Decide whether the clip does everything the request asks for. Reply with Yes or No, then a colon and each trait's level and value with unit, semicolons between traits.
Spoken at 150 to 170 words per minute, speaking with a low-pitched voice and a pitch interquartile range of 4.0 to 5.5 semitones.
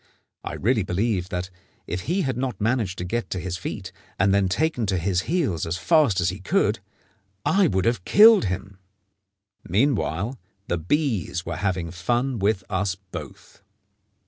Yes: average, 165 wpm; low, 100 Hz; average, 5.2 semitones